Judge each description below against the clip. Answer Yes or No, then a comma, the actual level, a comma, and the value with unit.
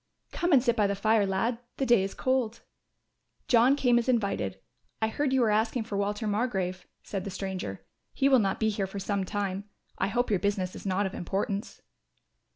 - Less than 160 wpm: No, average, 195 wpm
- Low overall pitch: No, high, 205 Hz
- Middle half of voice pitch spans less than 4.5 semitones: Yes, average, 3.6 semitones